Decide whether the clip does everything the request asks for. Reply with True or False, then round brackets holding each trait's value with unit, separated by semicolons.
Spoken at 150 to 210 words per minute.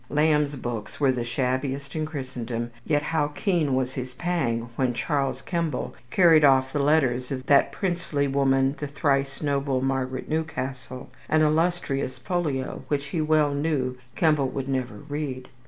True (155 wpm)